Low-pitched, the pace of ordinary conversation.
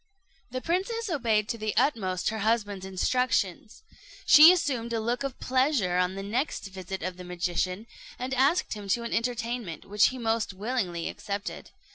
No: high, 225 Hz; average, 165 wpm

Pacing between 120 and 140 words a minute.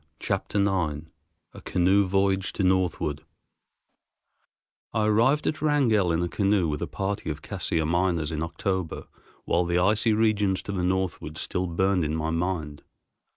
No: average, 155 wpm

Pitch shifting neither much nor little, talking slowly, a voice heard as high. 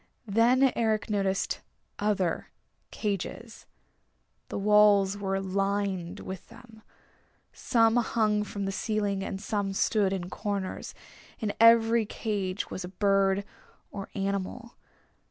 No: narrow, 2.2 semitones; slow, 115 wpm; high, 205 Hz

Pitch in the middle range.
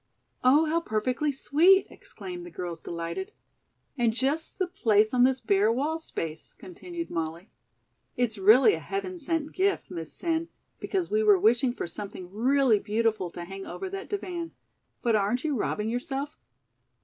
No: very high, 260 Hz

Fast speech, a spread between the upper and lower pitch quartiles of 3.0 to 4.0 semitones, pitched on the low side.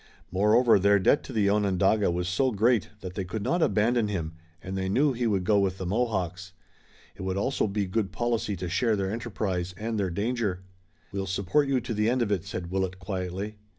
Yes: fast, 210 wpm; average, 3.3 semitones; low, 100 Hz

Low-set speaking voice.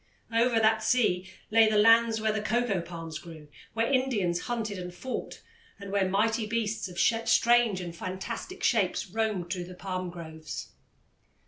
No: high, 210 Hz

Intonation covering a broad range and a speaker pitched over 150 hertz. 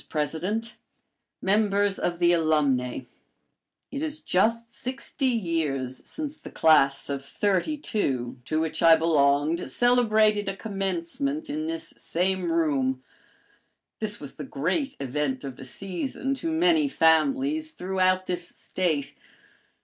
Yes: wide, 8.1 semitones; medium, 185 Hz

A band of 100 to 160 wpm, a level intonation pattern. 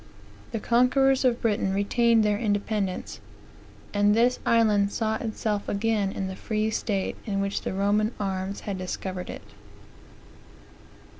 Yes: slow, 135 wpm; narrow, 2.3 semitones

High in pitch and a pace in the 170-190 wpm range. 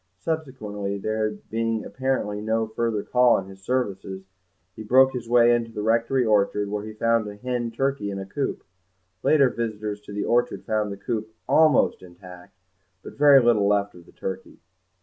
No: low, 110 Hz; average, 175 wpm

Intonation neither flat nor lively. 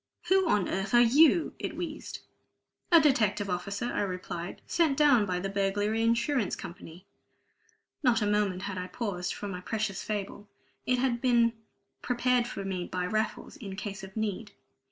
Yes: average, 3.8 semitones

